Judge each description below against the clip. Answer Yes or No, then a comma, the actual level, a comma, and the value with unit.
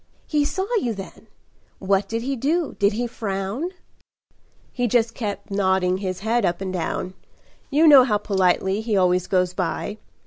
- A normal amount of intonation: Yes, average, 4.3 semitones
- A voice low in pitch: No, high, 205 Hz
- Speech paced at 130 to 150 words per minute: No, average, 165 wpm